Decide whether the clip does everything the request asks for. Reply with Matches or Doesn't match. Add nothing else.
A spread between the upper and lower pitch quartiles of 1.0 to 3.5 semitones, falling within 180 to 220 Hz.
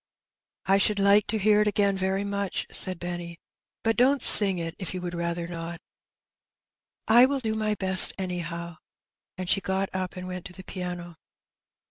Matches